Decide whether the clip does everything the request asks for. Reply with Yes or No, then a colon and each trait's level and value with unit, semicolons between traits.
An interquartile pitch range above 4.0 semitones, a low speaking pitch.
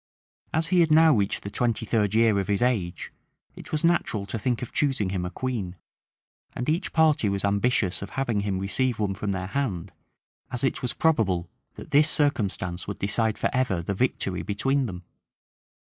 Yes: average, 5.0 semitones; low, 110 Hz